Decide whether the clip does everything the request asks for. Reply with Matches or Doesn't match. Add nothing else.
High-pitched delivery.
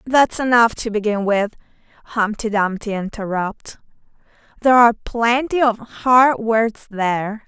Matches